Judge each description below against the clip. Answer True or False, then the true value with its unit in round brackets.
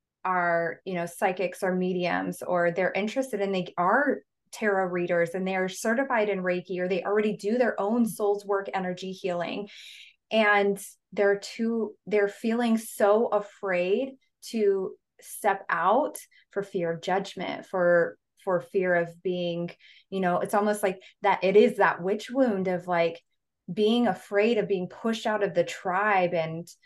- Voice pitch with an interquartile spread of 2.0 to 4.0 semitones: True (2.8 semitones)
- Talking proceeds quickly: False (160 wpm)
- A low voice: False (195 Hz)